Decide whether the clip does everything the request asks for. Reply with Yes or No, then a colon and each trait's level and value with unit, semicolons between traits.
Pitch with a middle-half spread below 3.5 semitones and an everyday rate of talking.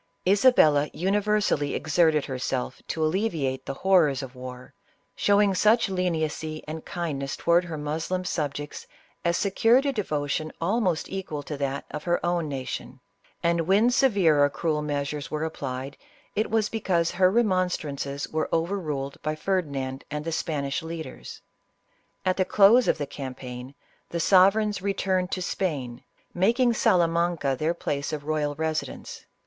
No: average, 4.7 semitones; average, 150 wpm